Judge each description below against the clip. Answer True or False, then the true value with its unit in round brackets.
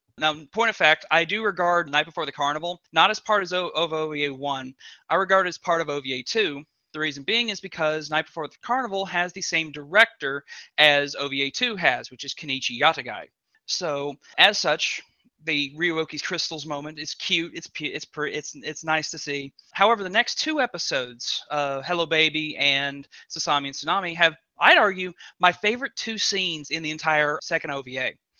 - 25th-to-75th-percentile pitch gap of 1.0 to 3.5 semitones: False (3.9 semitones)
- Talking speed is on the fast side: False (185 wpm)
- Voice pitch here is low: False (160 Hz)